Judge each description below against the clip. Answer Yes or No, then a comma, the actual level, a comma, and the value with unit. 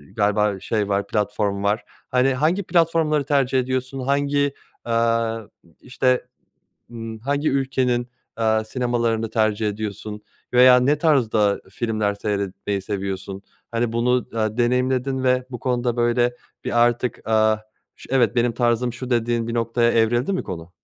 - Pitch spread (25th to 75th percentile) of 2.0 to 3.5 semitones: Yes, average, 2.8 semitones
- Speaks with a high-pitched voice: No, low, 120 Hz